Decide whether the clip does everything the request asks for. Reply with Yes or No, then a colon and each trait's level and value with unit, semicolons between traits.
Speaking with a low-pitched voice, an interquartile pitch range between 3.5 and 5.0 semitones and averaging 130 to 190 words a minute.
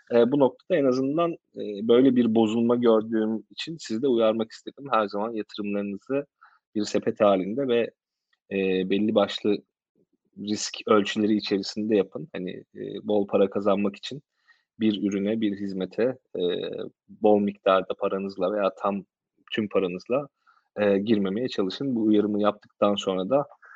No: low, 105 Hz; average, 2.7 semitones; fast, 140 wpm